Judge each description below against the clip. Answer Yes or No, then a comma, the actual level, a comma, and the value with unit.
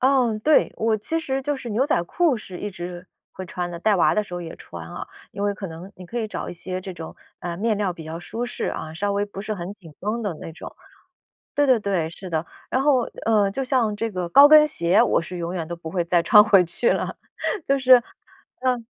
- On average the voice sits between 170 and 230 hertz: Yes, high, 200 Hz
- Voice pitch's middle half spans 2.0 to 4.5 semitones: No, average, 5.3 semitones